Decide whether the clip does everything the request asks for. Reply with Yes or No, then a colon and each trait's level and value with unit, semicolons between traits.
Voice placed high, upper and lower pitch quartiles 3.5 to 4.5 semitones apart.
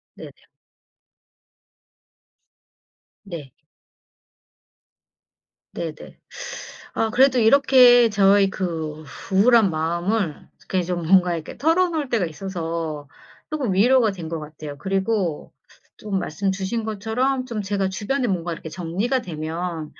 No: high, 195 Hz; wide, 5.5 semitones